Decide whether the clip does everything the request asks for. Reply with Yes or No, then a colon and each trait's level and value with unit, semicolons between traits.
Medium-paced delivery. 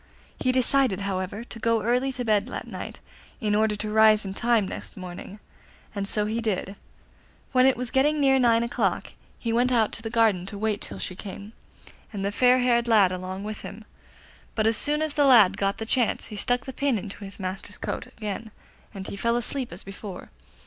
No: fast, 210 wpm